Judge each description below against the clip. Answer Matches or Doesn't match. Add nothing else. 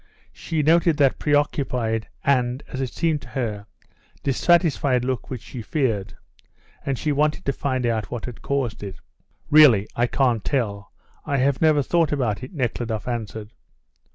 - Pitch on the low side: Matches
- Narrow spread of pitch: Doesn't match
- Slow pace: Doesn't match